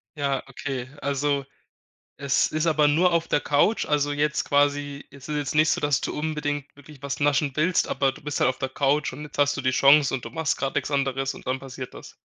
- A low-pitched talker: No, medium, 145 Hz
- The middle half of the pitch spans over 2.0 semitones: No, narrow, 1.6 semitones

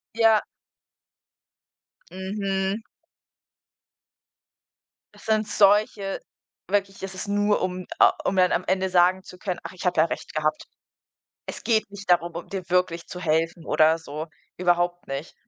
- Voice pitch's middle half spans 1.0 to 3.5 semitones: Yes, narrow, 2.4 semitones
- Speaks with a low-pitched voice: No, medium, 185 Hz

